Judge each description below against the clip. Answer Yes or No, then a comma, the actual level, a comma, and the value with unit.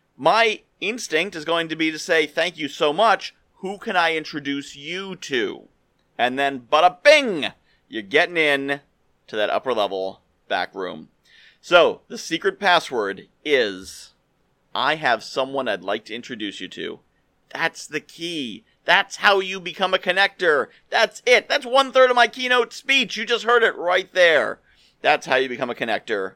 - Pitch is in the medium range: Yes, medium, 170 Hz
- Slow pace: No, average, 175 wpm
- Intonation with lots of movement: Yes, wide, 6.7 semitones